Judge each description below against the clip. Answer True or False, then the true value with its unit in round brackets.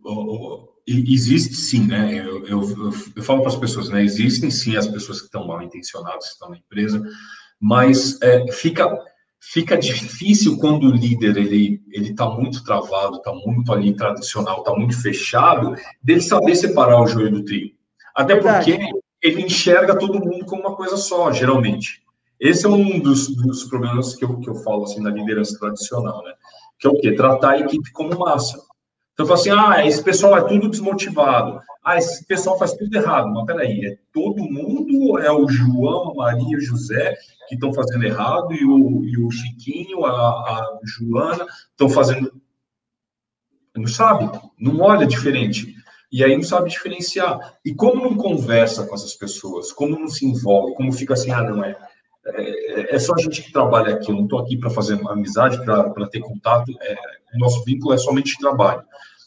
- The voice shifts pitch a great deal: True (6.5 semitones)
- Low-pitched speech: True (130 Hz)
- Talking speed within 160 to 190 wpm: True (185 wpm)